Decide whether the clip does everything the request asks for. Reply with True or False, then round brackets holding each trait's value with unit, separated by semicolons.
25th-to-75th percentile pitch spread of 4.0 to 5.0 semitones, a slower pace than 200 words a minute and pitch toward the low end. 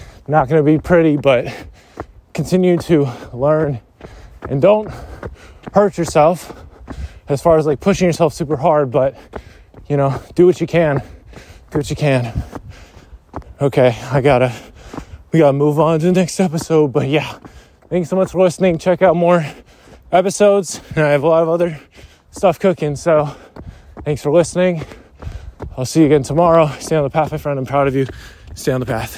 False (4.7 semitones; 180 wpm; 150 Hz)